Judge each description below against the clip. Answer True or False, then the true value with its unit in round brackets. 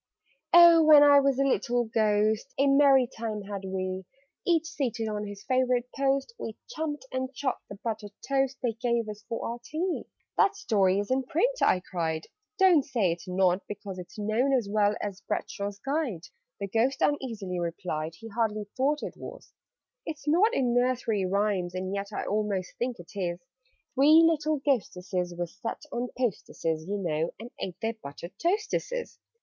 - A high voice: True (225 Hz)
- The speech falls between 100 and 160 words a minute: False (175 wpm)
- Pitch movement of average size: False (5.7 semitones)